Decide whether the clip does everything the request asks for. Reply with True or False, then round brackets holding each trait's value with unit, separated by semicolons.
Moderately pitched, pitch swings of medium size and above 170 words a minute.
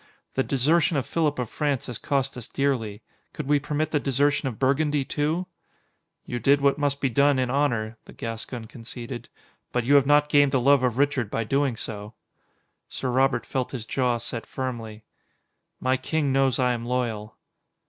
False (130 Hz; 3.0 semitones; 180 wpm)